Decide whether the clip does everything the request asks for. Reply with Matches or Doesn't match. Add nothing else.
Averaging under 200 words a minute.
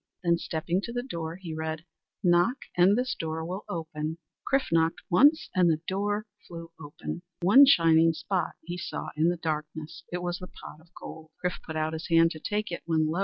Doesn't match